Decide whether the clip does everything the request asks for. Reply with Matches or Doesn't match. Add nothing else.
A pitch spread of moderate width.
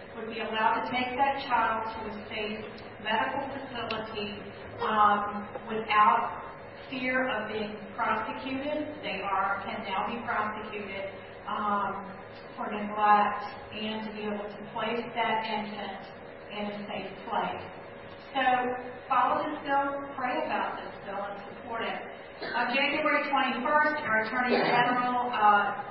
Matches